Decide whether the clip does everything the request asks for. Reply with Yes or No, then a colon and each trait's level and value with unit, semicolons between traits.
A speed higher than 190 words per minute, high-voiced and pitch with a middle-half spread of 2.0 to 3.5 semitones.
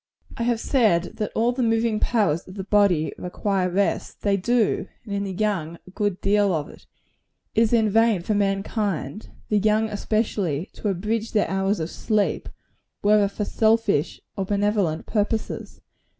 No: average, 165 wpm; high, 205 Hz; narrow, 2.4 semitones